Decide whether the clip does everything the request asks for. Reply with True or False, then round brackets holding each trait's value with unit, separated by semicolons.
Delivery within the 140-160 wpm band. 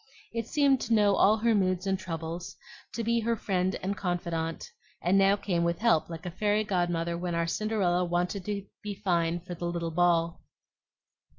False (185 wpm)